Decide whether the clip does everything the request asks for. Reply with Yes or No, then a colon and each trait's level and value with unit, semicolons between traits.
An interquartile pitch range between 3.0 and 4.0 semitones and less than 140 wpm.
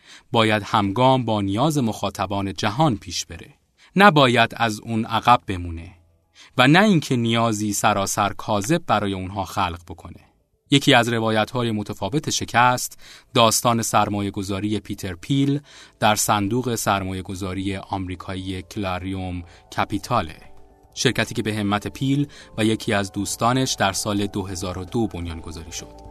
Yes: average, 3.4 semitones; average, 130 wpm